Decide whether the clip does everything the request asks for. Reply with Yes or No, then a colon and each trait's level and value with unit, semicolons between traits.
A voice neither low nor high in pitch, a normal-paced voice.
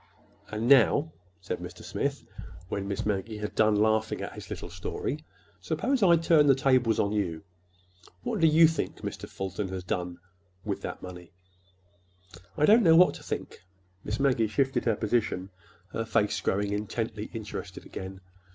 No: low, 110 Hz; average, 160 wpm